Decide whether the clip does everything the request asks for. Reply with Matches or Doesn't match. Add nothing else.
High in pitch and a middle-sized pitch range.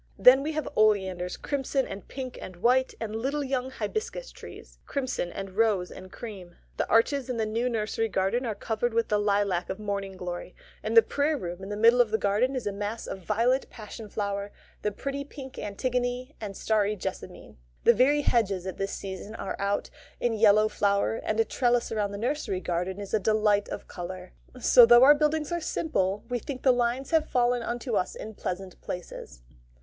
Matches